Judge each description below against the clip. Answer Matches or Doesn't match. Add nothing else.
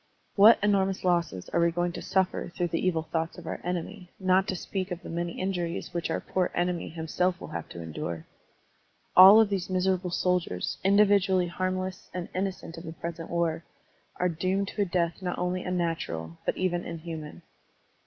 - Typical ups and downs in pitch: Doesn't match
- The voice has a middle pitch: Matches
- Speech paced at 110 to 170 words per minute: Doesn't match